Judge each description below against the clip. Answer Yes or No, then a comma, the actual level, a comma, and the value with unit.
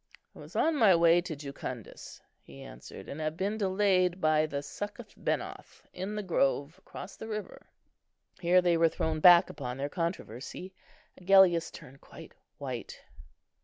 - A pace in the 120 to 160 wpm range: Yes, average, 155 wpm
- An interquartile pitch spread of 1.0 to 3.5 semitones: No, average, 4.6 semitones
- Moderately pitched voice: Yes, medium, 170 Hz